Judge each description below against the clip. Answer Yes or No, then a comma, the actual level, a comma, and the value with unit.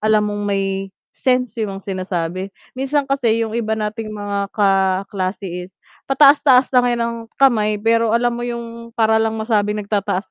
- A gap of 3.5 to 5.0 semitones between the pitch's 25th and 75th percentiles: No, average, 3.0 semitones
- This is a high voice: Yes, high, 220 Hz